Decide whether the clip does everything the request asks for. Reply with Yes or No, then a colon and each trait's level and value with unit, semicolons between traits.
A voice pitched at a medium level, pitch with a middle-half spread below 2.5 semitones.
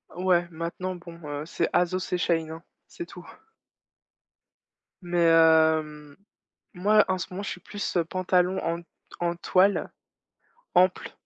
Yes: medium, 175 Hz; narrow, 2.0 semitones